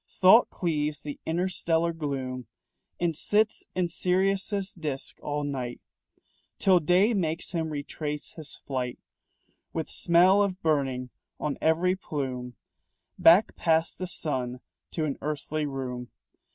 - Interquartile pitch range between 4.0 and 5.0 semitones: Yes, average, 4.3 semitones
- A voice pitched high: No, medium, 160 Hz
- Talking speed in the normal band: No, slow, 125 wpm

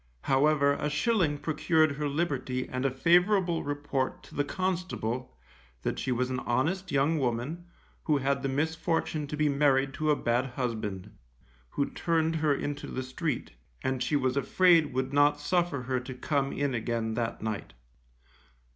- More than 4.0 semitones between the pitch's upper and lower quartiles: No, average, 3.4 semitones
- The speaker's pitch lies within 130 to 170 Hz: Yes, medium, 140 Hz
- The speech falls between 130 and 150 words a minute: No, average, 165 wpm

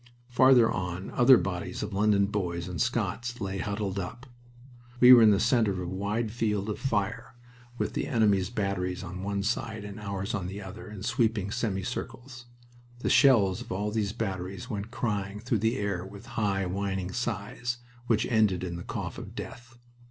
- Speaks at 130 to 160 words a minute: No, average, 180 wpm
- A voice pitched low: Yes, low, 105 Hz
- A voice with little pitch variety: No, average, 3.3 semitones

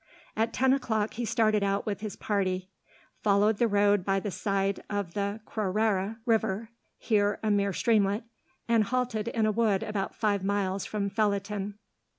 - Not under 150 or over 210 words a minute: Yes, average, 165 wpm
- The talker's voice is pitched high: Yes, high, 205 Hz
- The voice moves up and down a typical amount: No, narrow, 1.8 semitones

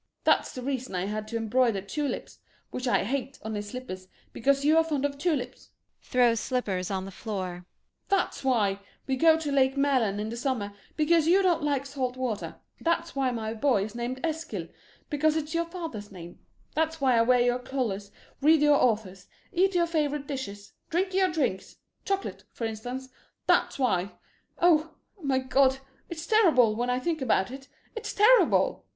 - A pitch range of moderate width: No, wide, 5.9 semitones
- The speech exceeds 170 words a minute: Yes, average, 180 wpm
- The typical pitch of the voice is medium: No, very high, 260 Hz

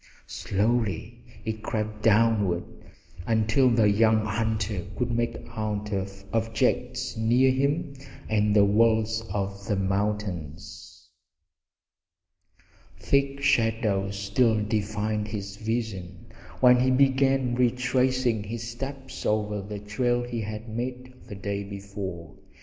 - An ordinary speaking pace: No, slow, 110 wpm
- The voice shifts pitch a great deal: No, average, 3.0 semitones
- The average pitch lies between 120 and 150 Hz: No, low, 110 Hz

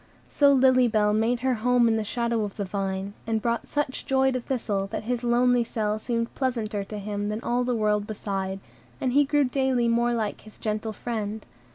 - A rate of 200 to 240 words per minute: Yes, fast, 205 wpm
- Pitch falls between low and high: No, high, 230 Hz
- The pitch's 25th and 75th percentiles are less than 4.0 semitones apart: Yes, average, 2.9 semitones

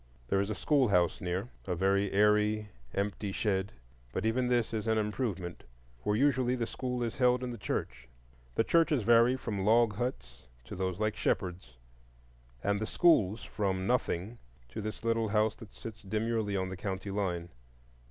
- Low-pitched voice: Yes, low, 105 Hz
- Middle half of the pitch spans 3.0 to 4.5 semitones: Yes, average, 3.4 semitones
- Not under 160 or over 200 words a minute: Yes, average, 165 wpm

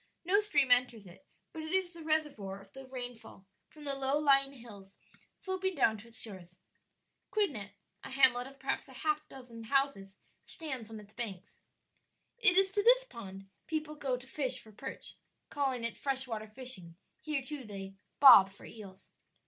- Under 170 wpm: No, average, 175 wpm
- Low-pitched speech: No, very high, 260 Hz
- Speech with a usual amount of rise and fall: No, wide, 5.8 semitones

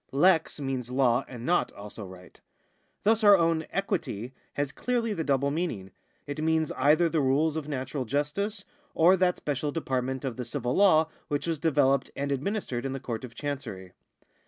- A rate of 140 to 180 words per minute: Yes, average, 175 wpm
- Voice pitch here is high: No, medium, 145 Hz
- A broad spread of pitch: No, average, 4.2 semitones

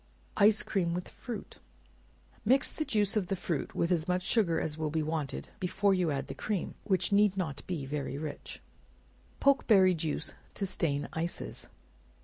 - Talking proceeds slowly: No, average, 165 wpm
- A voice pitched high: No, medium, 180 Hz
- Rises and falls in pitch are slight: No, average, 4.2 semitones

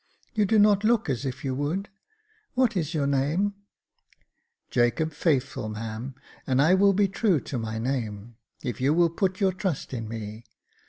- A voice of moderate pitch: Yes, medium, 145 Hz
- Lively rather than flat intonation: Yes, wide, 7.9 semitones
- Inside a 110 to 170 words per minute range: No, average, 180 wpm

